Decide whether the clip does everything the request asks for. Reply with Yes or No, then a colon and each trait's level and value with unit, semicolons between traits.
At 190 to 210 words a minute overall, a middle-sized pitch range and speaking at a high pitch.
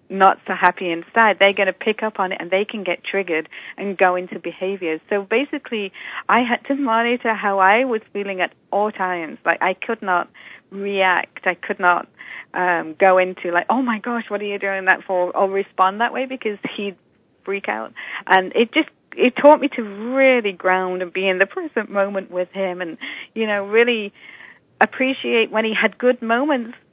Yes: average, 200 wpm; average, 3.7 semitones; high, 200 Hz